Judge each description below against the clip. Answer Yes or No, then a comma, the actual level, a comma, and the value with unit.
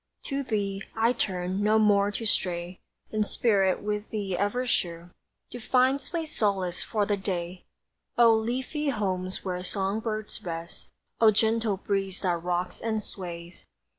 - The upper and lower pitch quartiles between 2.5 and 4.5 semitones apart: Yes, average, 3.4 semitones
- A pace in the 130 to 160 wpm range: Yes, average, 150 wpm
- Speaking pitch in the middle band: No, high, 205 Hz